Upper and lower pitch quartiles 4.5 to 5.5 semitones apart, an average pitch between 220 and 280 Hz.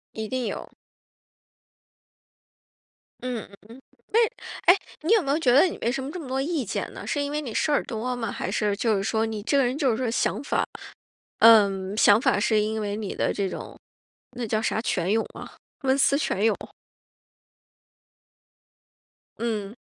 No: average, 4.1 semitones; high, 230 Hz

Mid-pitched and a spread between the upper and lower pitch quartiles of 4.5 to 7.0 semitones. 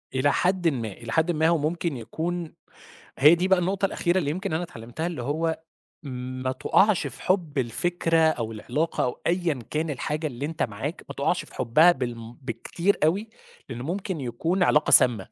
Yes: medium, 155 Hz; wide, 5.6 semitones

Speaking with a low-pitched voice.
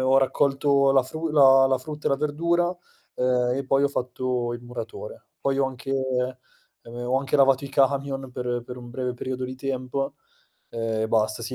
Yes: low, 130 Hz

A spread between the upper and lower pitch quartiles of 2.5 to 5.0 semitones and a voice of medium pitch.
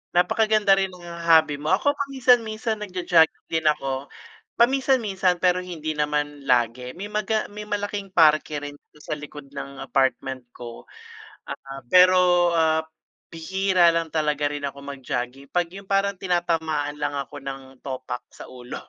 No: wide, 5.4 semitones; medium, 160 Hz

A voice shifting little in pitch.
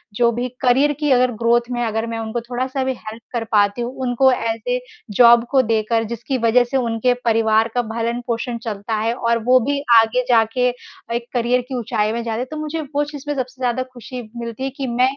Yes: narrow, 2.0 semitones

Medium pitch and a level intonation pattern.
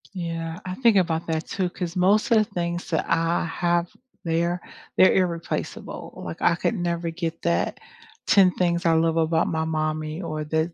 Yes: medium, 170 Hz; narrow, 1.7 semitones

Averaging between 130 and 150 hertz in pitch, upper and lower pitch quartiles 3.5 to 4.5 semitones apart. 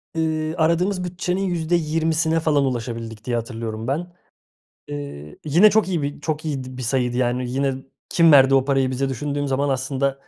Yes: medium, 140 Hz; average, 4.1 semitones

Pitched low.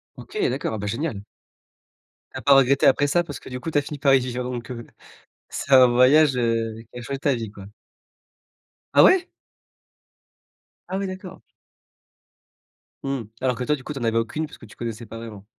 Yes: low, 125 Hz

